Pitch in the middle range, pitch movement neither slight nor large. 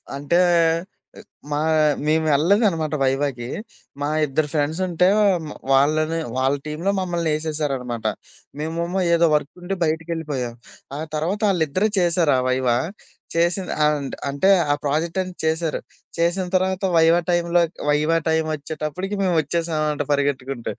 Yes: medium, 160 Hz; average, 3.0 semitones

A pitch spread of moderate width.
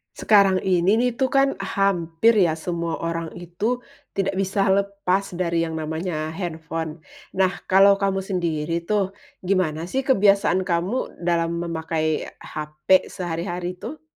Yes: average, 3.0 semitones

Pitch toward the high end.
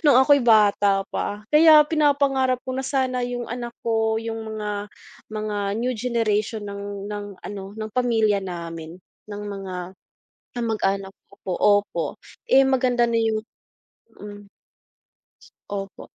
Yes: high, 220 Hz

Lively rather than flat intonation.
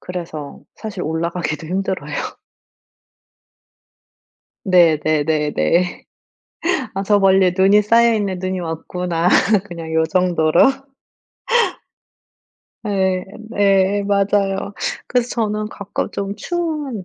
No: average, 3.4 semitones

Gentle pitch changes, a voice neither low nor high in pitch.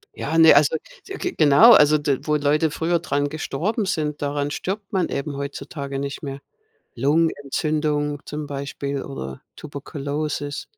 Yes: narrow, 1.9 semitones; medium, 145 Hz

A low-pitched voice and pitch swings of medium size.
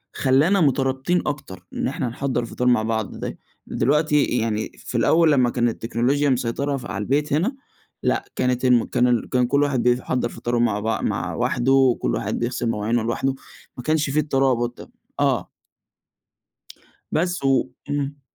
Yes: low, 130 Hz; average, 3.1 semitones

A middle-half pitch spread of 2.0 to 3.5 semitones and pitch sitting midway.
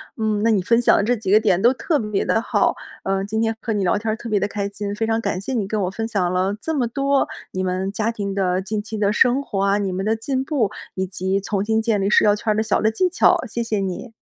No: narrow, 2.5 semitones; high, 210 Hz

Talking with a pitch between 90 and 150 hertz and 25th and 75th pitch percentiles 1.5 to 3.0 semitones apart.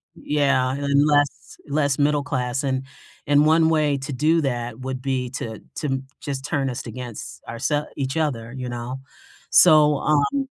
Yes: medium, 140 Hz; narrow, 2.5 semitones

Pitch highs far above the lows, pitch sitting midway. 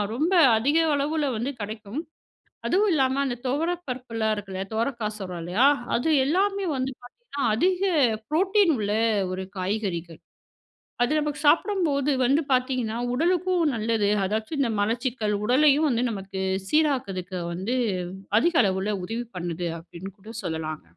No: wide, 6.7 semitones; high, 245 Hz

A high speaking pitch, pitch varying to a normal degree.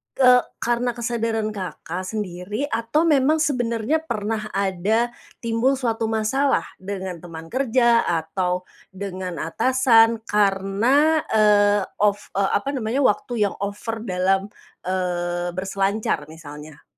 Yes: high, 210 Hz; average, 4.2 semitones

